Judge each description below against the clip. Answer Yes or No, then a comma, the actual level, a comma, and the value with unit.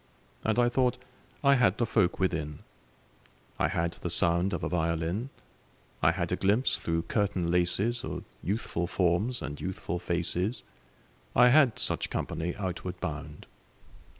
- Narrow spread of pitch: No, average, 4.8 semitones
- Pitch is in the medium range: No, very low, 90 Hz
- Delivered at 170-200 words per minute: No, average, 145 wpm